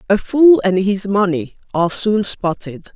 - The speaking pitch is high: Yes, high, 200 Hz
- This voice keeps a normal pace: Yes, average, 165 wpm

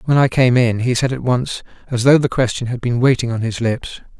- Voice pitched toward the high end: No, low, 125 Hz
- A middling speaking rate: No, fast, 255 wpm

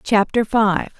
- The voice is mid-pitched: No, high, 215 Hz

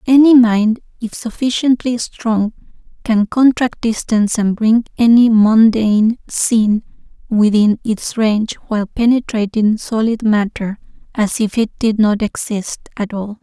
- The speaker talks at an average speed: No, slow, 125 wpm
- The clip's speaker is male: No, female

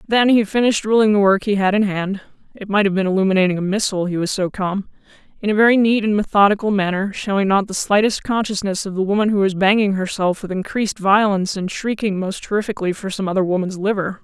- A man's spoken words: No, female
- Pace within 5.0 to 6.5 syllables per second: Yes, 5.4 syllables/s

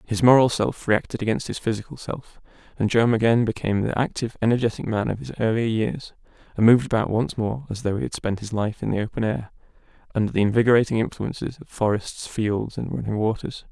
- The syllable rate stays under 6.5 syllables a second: Yes, 6.1 syllables/s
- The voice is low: Yes, low, 110 Hz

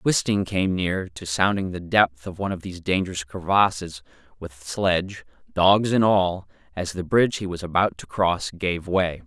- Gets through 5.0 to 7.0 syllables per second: No, 4.7 syllables/s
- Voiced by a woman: No, male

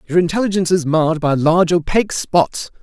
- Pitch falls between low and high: Yes, medium, 170 Hz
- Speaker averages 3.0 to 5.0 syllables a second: No, 6.1 syllables/s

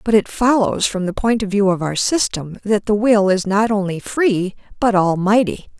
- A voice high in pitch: Yes, high, 205 Hz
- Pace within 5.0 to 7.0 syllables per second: No, 4.7 syllables/s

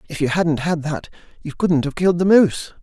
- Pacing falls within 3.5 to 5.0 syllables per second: No, 5.9 syllables/s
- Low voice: No, medium, 160 Hz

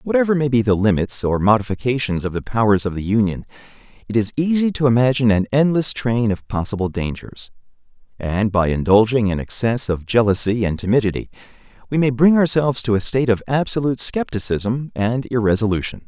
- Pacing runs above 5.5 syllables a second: Yes, 5.9 syllables/s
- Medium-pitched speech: No, low, 115 Hz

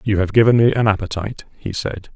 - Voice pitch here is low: Yes, low, 105 Hz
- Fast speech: Yes, fast, 220 wpm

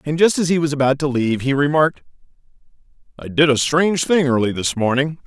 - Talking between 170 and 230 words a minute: Yes, fast, 205 wpm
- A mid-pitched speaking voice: Yes, medium, 145 Hz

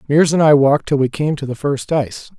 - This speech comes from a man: Yes, male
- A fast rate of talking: Yes, fast, 275 wpm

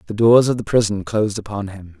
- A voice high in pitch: No, low, 105 Hz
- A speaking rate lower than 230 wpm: No, fast, 240 wpm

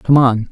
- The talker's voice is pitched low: Yes, low, 125 Hz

